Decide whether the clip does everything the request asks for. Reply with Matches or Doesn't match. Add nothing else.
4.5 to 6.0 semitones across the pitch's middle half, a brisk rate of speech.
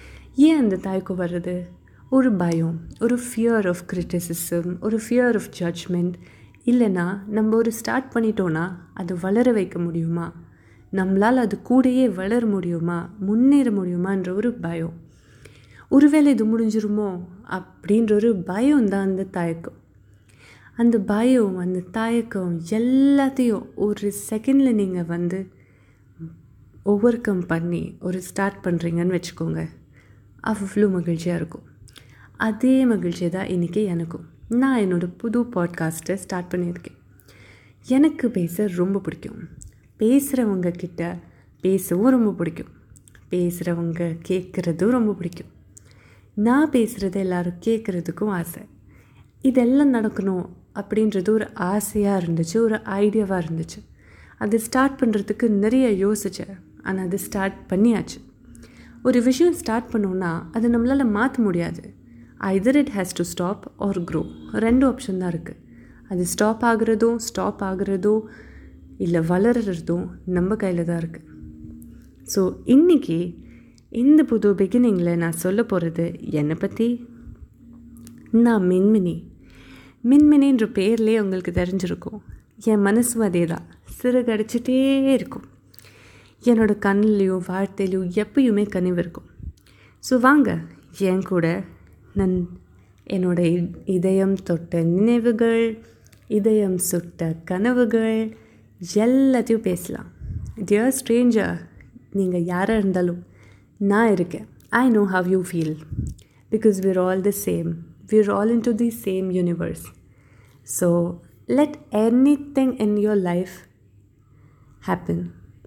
Doesn't match